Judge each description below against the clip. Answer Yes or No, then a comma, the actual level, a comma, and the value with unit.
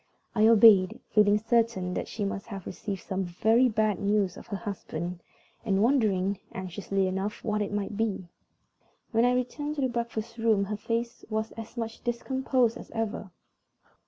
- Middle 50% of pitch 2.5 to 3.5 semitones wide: Yes, average, 2.8 semitones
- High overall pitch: Yes, high, 215 Hz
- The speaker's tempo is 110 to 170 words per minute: Yes, average, 165 wpm